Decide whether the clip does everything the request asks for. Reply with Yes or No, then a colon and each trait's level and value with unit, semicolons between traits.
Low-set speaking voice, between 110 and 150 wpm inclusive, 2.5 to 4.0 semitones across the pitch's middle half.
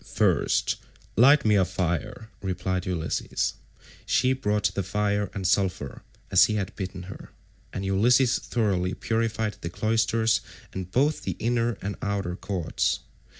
Yes: low, 100 Hz; average, 140 wpm; average, 3.3 semitones